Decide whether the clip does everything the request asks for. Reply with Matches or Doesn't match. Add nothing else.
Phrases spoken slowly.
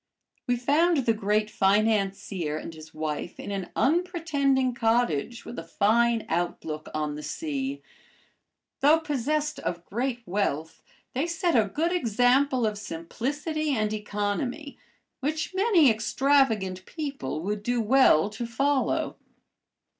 Matches